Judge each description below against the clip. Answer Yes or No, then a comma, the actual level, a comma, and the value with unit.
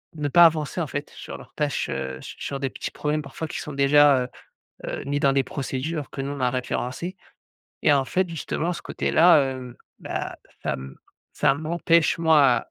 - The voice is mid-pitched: Yes, medium, 145 Hz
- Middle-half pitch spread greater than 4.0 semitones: No, average, 3.0 semitones